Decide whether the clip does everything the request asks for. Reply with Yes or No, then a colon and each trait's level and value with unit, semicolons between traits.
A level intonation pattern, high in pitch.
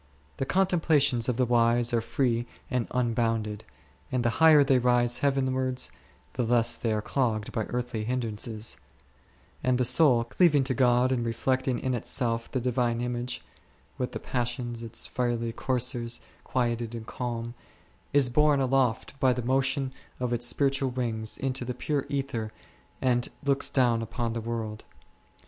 No: narrow, 2.0 semitones; low, 125 Hz